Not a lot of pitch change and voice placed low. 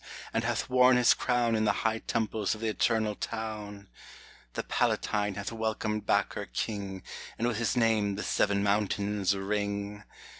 Yes: narrow, 1.8 semitones; low, 105 Hz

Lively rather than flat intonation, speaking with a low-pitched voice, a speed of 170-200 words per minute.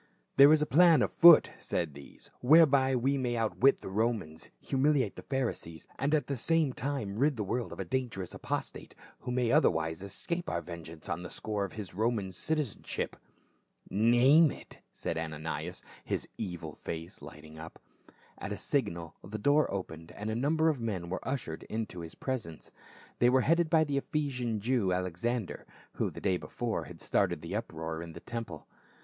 Yes: wide, 7.8 semitones; low, 115 Hz; average, 185 wpm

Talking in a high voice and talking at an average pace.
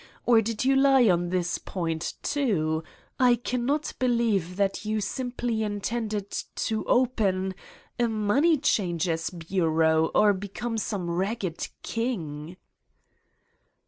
No: high, 205 Hz; slow, 110 wpm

